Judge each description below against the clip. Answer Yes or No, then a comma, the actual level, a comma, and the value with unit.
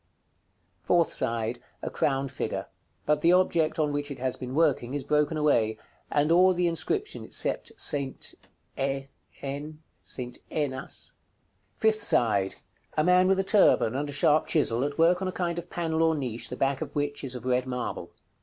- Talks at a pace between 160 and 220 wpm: Yes, average, 170 wpm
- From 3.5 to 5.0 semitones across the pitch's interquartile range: Yes, average, 4.3 semitones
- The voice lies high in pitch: No, medium, 145 Hz